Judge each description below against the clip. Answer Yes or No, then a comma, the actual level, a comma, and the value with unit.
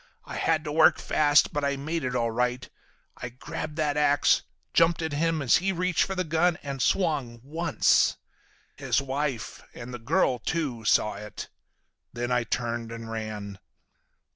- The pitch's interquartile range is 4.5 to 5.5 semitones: Yes, average, 5.1 semitones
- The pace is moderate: Yes, average, 165 wpm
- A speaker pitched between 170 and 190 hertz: No, medium, 140 Hz